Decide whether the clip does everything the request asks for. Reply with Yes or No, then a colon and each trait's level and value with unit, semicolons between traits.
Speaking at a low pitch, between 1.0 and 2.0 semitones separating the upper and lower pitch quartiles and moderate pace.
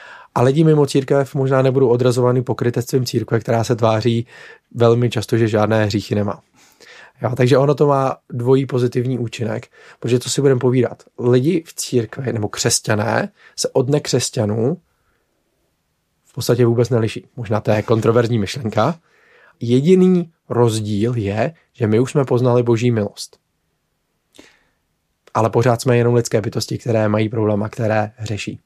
No: low, 120 Hz; narrow, 2.6 semitones; average, 145 wpm